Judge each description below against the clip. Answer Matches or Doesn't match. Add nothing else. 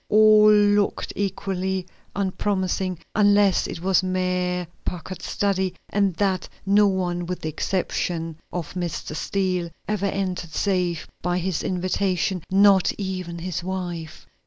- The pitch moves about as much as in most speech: Doesn't match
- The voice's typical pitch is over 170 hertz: Matches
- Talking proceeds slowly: Matches